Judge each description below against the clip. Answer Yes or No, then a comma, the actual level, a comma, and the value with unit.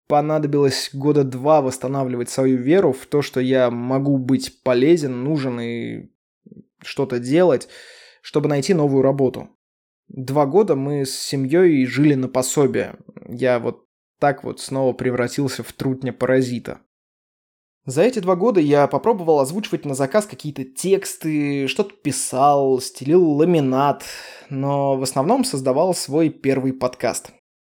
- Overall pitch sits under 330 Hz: Yes, medium, 140 Hz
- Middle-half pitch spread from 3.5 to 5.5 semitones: No, average, 2.9 semitones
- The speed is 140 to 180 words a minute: No, average, 130 wpm